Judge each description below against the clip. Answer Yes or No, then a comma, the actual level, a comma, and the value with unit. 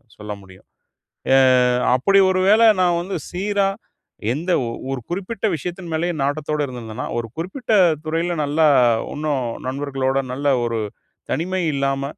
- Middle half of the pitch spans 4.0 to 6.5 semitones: Yes, average, 4.9 semitones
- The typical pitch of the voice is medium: Yes, medium, 155 Hz